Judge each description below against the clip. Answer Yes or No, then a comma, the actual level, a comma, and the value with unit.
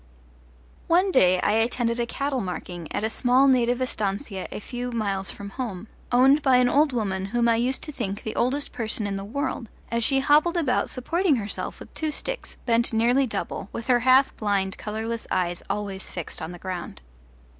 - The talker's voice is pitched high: Yes, high, 235 Hz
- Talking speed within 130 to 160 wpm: No, average, 190 wpm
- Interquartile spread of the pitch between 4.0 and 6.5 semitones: Yes, average, 4.6 semitones